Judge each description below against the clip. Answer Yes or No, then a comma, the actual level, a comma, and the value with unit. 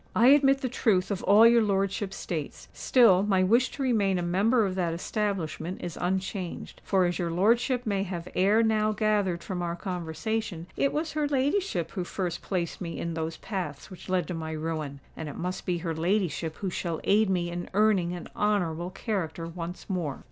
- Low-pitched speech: No, medium, 185 Hz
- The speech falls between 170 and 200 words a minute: Yes, average, 190 wpm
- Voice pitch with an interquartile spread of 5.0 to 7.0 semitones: No, average, 3.9 semitones